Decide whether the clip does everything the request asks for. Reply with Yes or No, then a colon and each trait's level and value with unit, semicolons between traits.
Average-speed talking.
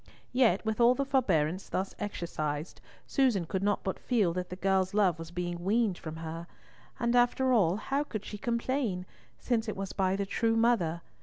Yes: average, 185 wpm